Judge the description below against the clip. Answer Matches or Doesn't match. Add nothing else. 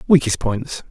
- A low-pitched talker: Matches